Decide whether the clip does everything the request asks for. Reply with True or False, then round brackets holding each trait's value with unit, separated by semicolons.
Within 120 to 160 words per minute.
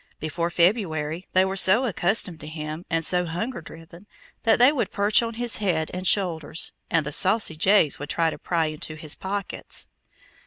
False (185 wpm)